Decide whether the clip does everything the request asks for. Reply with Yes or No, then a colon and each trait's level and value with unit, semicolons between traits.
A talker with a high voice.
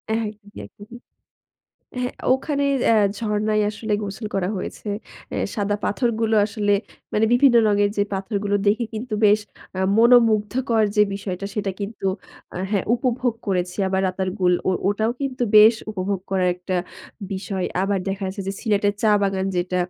Yes: high, 205 Hz